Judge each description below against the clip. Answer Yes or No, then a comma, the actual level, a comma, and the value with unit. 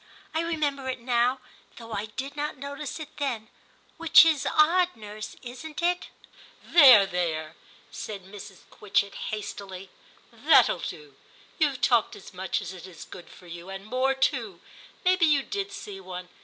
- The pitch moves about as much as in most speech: No, wide, 7.4 semitones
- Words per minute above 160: No, average, 155 wpm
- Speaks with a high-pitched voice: Yes, high, 240 Hz